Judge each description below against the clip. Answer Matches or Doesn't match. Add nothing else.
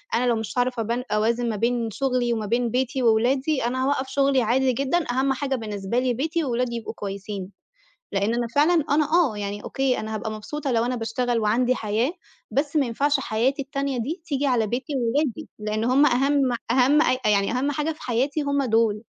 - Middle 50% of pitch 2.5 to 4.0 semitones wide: Matches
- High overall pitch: Matches